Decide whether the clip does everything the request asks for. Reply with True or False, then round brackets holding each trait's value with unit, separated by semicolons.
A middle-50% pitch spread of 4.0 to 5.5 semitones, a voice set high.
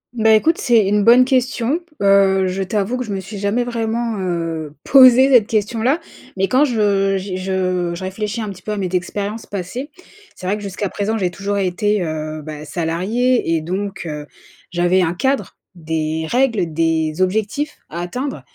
True (4.3 semitones; 200 Hz)